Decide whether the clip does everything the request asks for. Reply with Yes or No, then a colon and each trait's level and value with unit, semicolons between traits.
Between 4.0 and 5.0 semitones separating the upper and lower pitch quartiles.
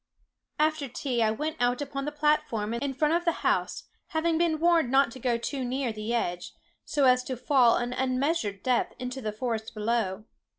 Yes: average, 4.3 semitones